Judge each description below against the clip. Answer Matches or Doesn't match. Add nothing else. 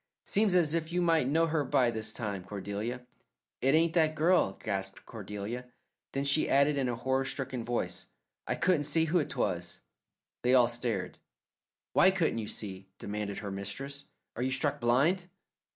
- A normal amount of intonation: Doesn't match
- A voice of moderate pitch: Doesn't match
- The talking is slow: Doesn't match